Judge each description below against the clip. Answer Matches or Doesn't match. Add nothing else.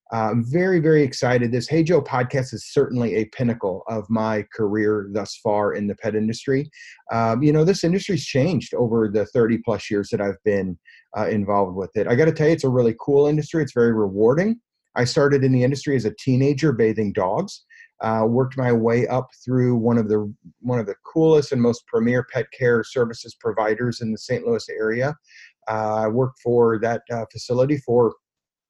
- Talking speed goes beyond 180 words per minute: Matches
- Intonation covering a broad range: Doesn't match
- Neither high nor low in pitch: Doesn't match